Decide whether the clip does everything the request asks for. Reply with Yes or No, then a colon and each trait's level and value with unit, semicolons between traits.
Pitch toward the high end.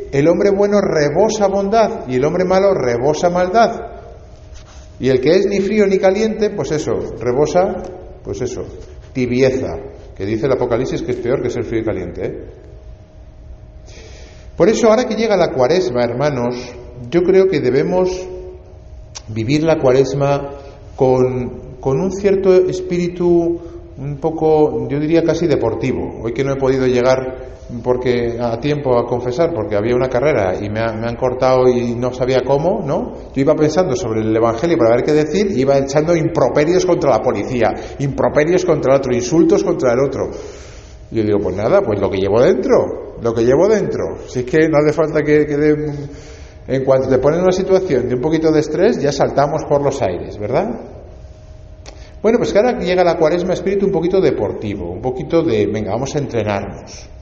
No: medium, 140 Hz